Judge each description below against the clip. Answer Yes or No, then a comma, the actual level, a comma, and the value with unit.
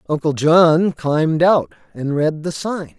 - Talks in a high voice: No, medium, 160 Hz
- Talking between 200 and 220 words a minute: No, average, 160 wpm